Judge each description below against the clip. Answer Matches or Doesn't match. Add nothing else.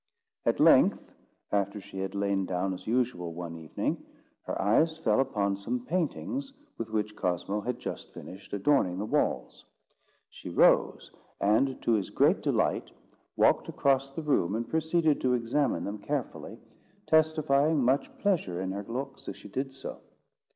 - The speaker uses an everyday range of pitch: Doesn't match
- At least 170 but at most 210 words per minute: Doesn't match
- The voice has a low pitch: Matches